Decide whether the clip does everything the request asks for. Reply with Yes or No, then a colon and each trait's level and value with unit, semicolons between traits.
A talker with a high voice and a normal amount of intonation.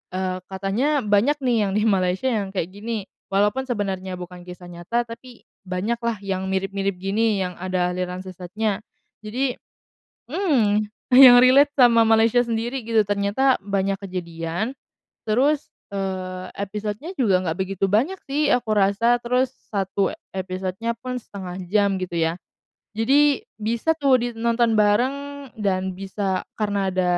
Yes: high, 205 Hz; average, 4.2 semitones